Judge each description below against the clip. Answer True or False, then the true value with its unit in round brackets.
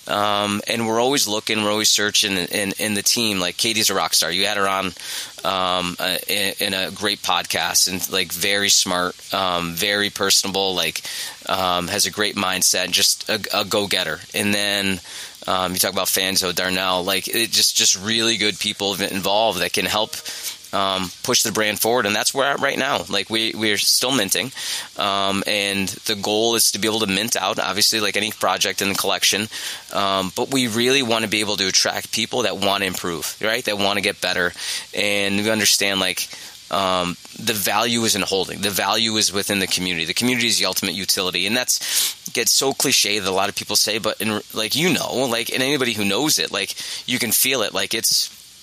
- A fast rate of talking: True (210 wpm)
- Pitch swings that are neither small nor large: False (2.2 semitones)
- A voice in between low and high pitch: False (100 Hz)